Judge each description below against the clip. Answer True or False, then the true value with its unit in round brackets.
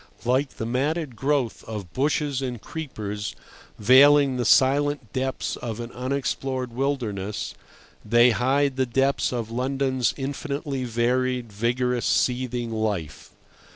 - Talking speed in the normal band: False (120 wpm)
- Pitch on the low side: True (125 Hz)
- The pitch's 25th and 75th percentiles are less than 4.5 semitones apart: True (2.7 semitones)